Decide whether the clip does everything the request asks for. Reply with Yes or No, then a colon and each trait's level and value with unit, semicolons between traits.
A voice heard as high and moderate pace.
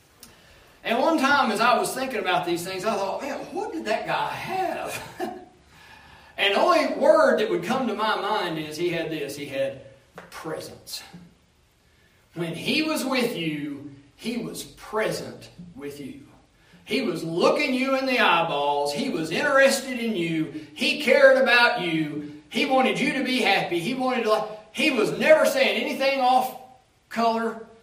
Yes: high, 230 Hz; average, 165 wpm